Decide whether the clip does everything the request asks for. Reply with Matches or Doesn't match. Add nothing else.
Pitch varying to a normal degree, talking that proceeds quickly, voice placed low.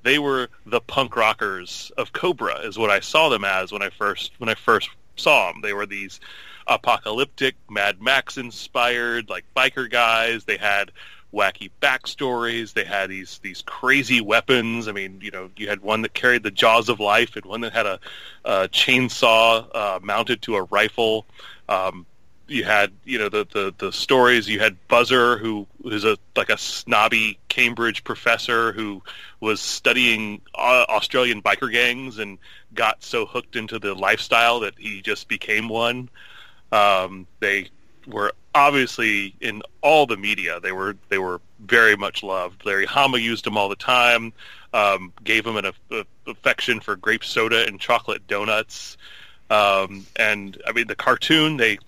Doesn't match